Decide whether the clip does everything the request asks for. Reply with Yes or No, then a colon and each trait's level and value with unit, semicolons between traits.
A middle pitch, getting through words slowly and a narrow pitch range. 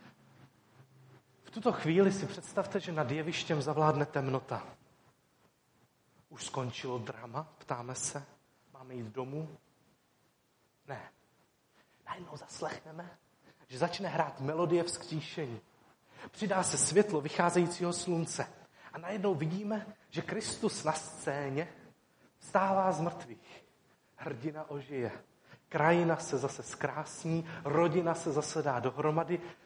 No: medium, 155 Hz; slow, 105 wpm; average, 3.7 semitones